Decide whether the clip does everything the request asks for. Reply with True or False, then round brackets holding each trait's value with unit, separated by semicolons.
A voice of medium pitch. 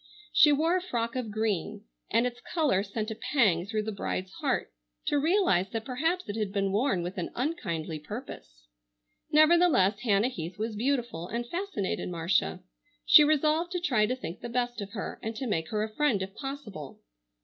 False (225 Hz)